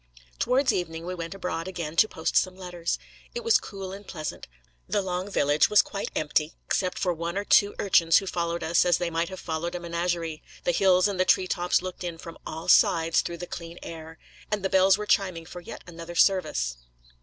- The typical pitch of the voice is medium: Yes, medium, 175 Hz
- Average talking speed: No, fast, 210 wpm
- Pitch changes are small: Yes, narrow, 2.3 semitones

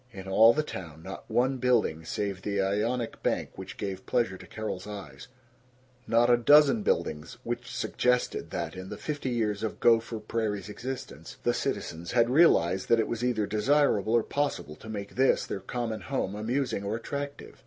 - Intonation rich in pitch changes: No, average, 4.0 semitones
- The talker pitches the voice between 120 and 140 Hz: No, low, 110 Hz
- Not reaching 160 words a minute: No, average, 175 wpm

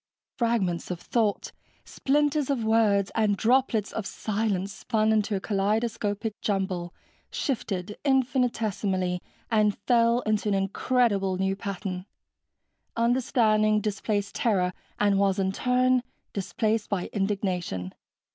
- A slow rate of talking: Yes, slow, 110 wpm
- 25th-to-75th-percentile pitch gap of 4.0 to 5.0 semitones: No, average, 3.1 semitones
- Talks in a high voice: Yes, high, 210 Hz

